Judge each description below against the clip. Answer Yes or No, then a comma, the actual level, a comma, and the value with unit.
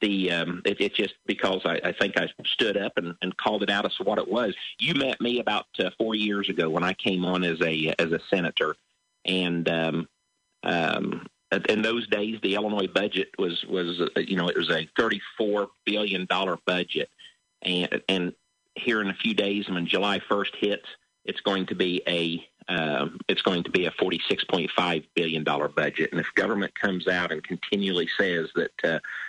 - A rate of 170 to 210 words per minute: Yes, average, 200 wpm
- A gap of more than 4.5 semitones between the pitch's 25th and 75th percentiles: No, average, 3.4 semitones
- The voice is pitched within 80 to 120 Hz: Yes, very low, 95 Hz